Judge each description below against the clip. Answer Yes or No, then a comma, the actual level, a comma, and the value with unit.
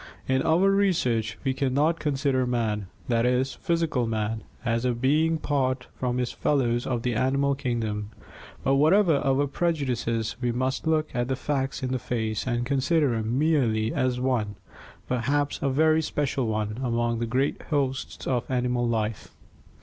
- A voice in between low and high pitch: No, low, 130 Hz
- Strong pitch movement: No, average, 3.3 semitones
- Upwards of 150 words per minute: Yes, average, 160 wpm